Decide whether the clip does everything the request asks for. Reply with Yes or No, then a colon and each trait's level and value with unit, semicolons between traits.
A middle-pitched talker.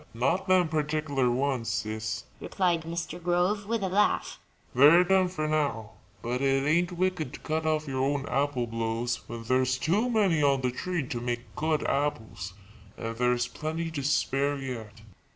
Yes: medium, 145 Hz